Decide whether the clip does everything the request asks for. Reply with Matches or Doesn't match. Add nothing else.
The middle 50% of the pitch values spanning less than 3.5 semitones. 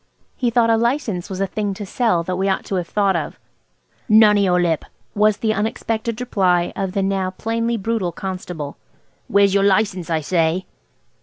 Matches